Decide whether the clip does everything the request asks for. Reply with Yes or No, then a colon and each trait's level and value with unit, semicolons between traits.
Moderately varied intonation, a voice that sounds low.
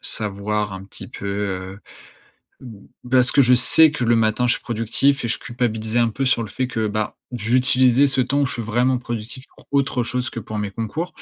Yes: average, 3.1 semitones; low, 120 Hz